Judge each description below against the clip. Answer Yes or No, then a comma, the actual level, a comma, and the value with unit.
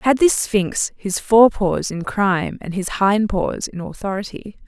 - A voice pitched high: Yes, high, 205 Hz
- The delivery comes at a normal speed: Yes, average, 180 wpm